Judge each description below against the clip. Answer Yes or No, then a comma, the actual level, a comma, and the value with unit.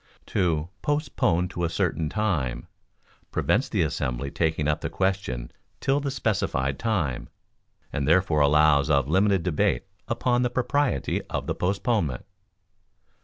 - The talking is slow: Yes, slow, 130 wpm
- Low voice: Yes, very low, 85 Hz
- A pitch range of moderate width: No, wide, 6.9 semitones